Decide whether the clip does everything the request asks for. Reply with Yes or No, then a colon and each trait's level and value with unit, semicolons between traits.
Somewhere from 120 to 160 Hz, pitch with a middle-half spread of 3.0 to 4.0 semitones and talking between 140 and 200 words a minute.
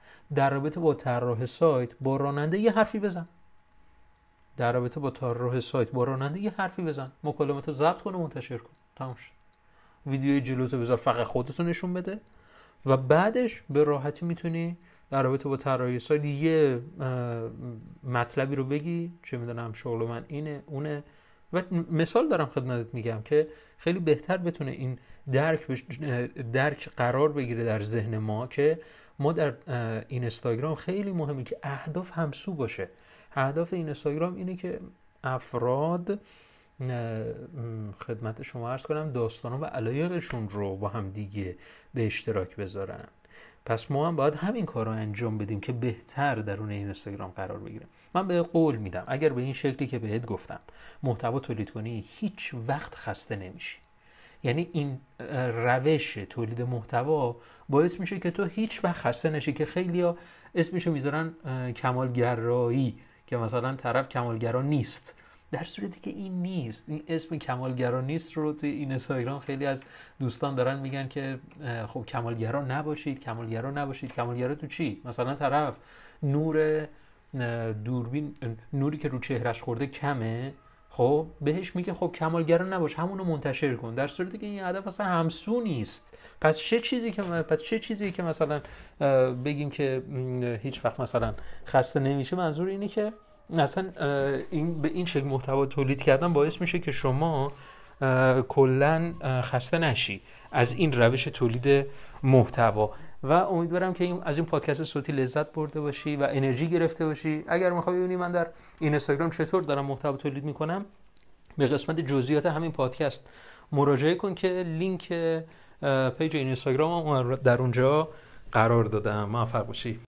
No: medium, 140 Hz; average, 4.7 semitones; average, 150 wpm